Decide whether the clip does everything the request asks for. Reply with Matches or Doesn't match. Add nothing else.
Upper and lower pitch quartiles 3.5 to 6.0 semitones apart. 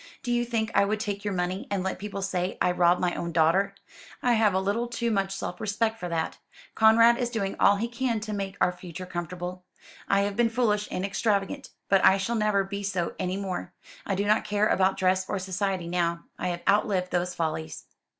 Doesn't match